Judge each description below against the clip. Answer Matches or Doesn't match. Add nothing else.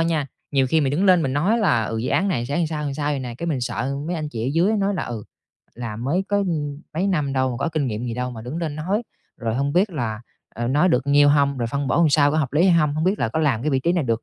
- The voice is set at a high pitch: Doesn't match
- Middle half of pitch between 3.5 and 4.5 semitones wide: Doesn't match